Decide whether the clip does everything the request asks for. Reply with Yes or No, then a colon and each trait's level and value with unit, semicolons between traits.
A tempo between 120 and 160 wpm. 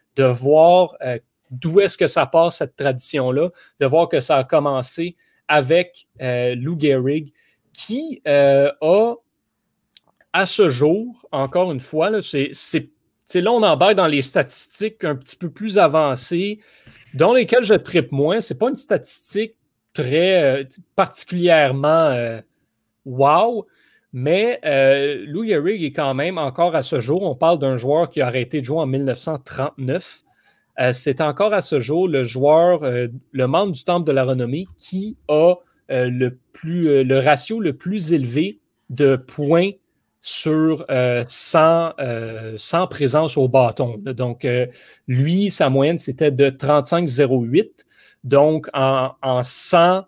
Yes: average, 155 wpm